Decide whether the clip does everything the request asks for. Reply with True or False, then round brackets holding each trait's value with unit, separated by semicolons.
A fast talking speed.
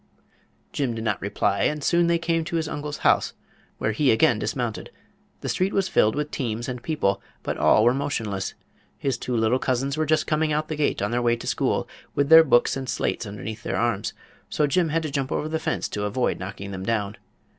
True (220 wpm)